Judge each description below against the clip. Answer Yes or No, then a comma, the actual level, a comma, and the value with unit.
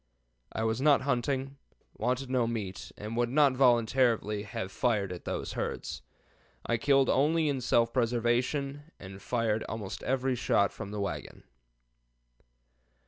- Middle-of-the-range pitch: No, low, 120 Hz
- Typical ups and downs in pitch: Yes, average, 3.8 semitones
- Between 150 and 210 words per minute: No, average, 140 wpm